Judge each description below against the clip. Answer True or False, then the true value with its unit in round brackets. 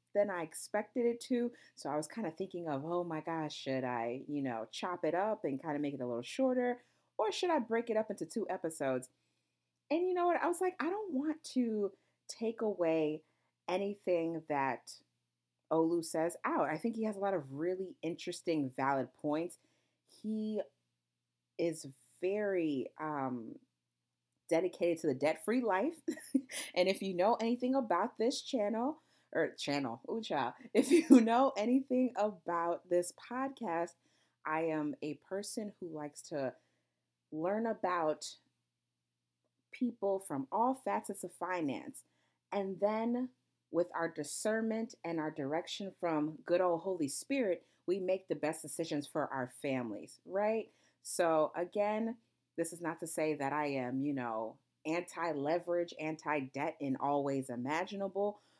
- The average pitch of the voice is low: False (170 Hz)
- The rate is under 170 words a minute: True (155 wpm)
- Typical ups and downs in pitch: False (6.8 semitones)